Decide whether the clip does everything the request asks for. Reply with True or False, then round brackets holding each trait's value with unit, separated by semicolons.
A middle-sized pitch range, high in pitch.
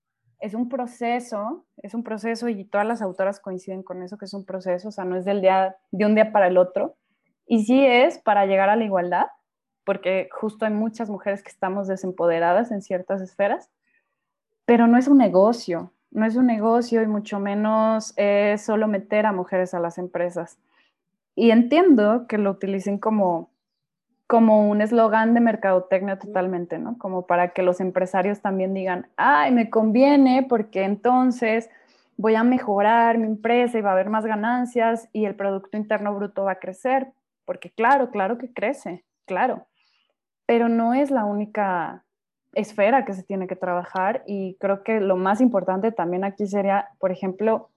True (3.4 semitones; 205 Hz)